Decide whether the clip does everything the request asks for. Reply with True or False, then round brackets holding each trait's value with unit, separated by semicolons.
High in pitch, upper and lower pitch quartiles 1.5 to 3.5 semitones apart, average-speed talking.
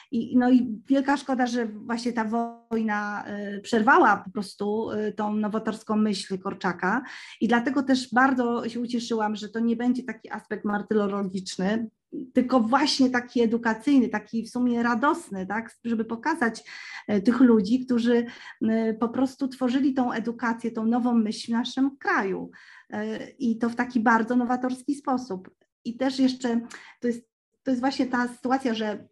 True (235 Hz; 2.6 semitones; 150 wpm)